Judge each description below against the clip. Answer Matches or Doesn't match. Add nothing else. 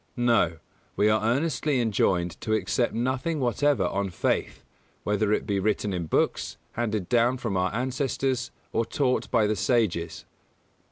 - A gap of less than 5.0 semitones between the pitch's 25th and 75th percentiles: Matches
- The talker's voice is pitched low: Matches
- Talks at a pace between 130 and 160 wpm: Matches